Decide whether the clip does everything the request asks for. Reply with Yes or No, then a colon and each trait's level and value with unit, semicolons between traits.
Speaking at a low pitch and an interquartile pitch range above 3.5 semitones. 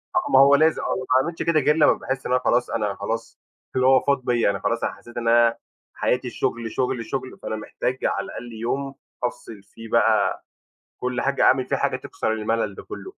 No: low, 125 Hz; average, 2.9 semitones